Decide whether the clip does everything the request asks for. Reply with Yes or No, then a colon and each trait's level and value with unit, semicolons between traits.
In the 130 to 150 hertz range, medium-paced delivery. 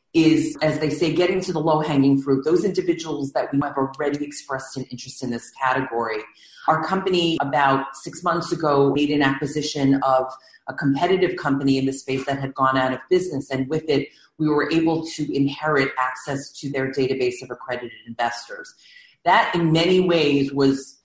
Yes: medium, 140 Hz; average, 185 wpm